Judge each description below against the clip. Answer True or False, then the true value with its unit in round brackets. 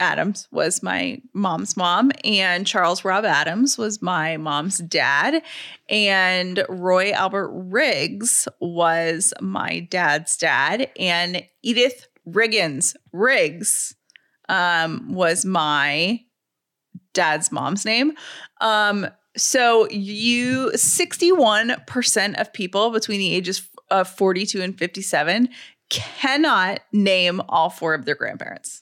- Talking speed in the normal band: False (105 wpm)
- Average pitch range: True (4.3 semitones)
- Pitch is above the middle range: True (195 Hz)